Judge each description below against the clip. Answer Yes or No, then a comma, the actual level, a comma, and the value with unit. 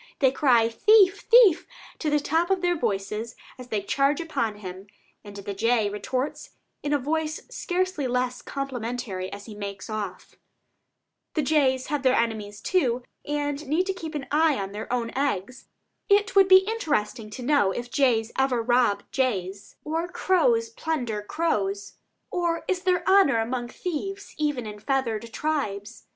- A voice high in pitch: Yes, very high, 260 Hz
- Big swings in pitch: Yes, wide, 6.7 semitones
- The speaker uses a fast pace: No, average, 165 wpm